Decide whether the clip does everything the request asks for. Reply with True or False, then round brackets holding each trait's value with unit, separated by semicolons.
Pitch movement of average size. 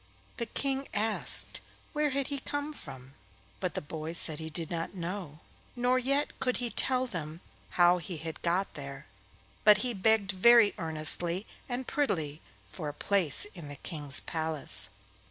False (7.4 semitones)